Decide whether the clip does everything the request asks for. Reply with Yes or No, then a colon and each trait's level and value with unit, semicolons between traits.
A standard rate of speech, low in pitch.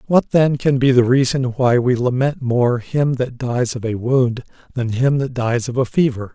No: fast, 215 wpm; low, 125 Hz